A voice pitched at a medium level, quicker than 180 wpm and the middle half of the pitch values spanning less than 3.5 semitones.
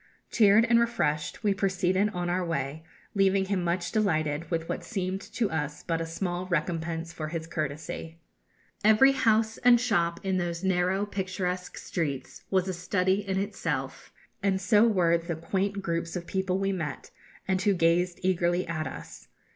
No: medium, 180 Hz; average, 165 wpm; average, 2.8 semitones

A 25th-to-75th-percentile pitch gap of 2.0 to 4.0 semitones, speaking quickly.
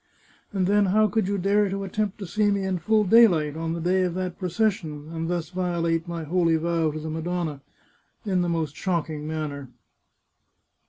No: average, 3.4 semitones; average, 190 wpm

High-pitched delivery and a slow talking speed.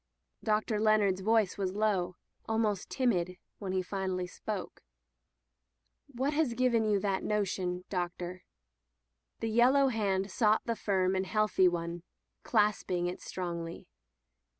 Yes: high, 200 Hz; slow, 125 wpm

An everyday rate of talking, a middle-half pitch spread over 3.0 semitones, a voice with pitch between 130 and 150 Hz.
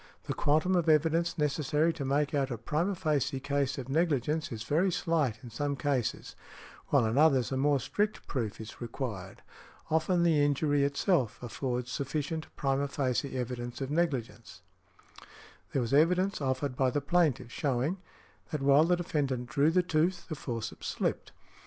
Yes: average, 160 wpm; average, 3.6 semitones; medium, 140 Hz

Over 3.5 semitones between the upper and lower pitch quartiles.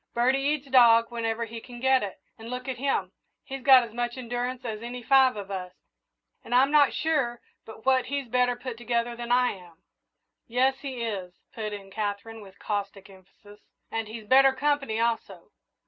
No: average, 3.1 semitones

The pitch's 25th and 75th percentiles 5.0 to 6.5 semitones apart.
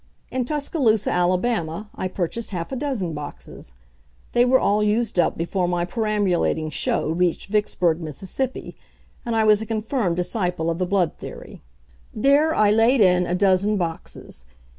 No: average, 4.3 semitones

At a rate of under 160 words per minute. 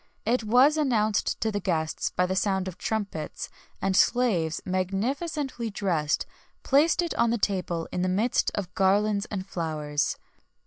Yes: average, 150 wpm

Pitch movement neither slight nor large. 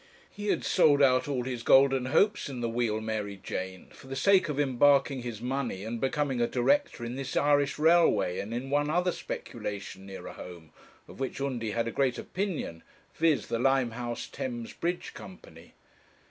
Yes: average, 4.0 semitones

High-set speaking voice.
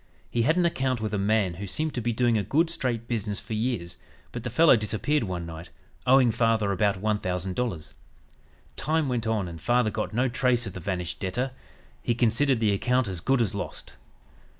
No: low, 115 Hz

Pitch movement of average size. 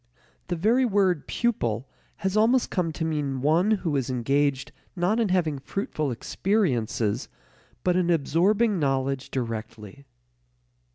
No: wide, 6.5 semitones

